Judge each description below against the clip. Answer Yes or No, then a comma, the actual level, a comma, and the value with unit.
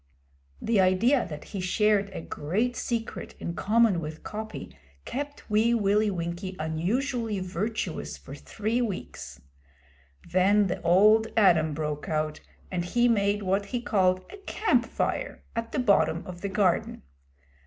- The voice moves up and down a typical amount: Yes, average, 4.2 semitones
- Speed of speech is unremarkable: Yes, average, 145 wpm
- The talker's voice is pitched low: No, high, 200 Hz